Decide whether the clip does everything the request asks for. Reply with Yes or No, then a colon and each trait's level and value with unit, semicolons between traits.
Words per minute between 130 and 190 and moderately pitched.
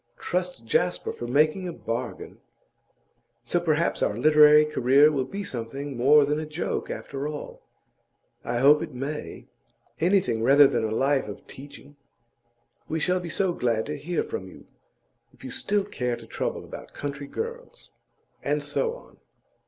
Yes: average, 160 wpm; medium, 150 Hz